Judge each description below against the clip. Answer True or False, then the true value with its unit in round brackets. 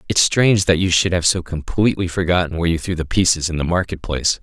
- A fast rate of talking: True (245 wpm)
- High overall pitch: False (85 Hz)